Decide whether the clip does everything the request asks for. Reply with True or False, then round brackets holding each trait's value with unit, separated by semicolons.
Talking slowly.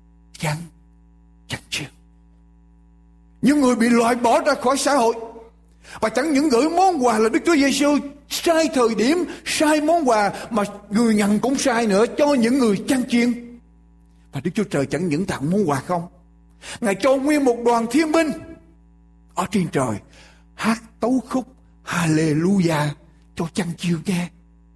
True (160 wpm)